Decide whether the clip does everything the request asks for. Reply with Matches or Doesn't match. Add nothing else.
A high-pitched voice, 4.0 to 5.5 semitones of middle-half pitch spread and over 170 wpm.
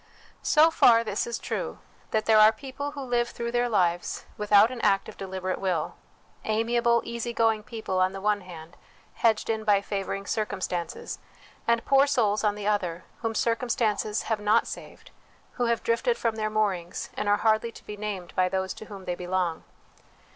Doesn't match